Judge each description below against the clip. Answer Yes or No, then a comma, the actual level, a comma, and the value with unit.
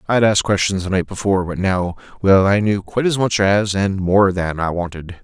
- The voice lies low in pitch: Yes, very low, 95 Hz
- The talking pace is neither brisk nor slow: No, fast, 220 wpm